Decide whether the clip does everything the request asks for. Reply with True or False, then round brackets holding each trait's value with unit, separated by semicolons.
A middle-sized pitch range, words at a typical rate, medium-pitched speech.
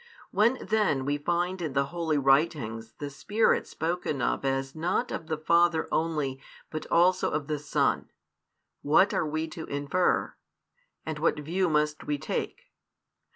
True (3.3 semitones; 155 wpm; 155 Hz)